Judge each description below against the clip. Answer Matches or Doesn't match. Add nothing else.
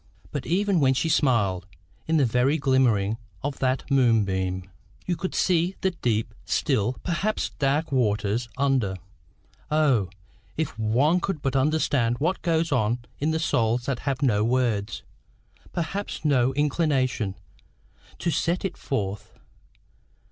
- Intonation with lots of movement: Matches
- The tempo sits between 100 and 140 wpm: Matches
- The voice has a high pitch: Doesn't match